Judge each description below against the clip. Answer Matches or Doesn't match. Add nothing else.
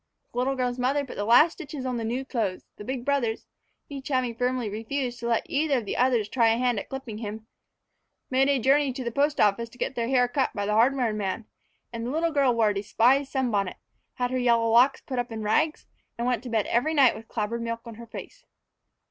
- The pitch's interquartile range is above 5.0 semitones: Doesn't match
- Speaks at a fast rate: Matches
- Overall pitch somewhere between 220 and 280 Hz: Matches